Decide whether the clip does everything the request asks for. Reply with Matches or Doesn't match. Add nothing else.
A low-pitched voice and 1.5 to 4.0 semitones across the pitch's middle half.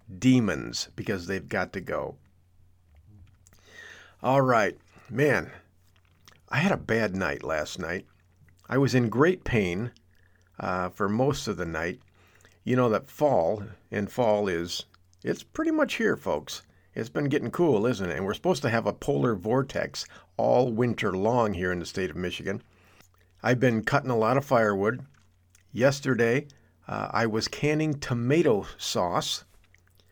Doesn't match